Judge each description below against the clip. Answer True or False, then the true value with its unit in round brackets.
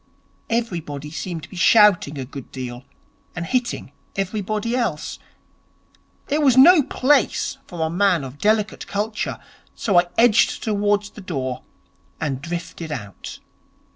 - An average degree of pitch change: False (6.6 semitones)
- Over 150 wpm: False (135 wpm)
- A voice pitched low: False (190 Hz)